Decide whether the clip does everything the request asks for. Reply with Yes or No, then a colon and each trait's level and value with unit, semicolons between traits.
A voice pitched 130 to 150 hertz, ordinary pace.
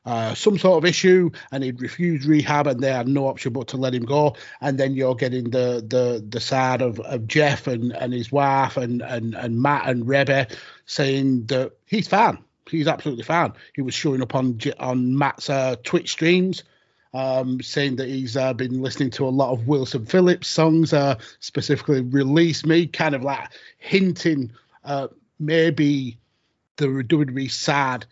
Yes: low, 135 Hz; average, 180 wpm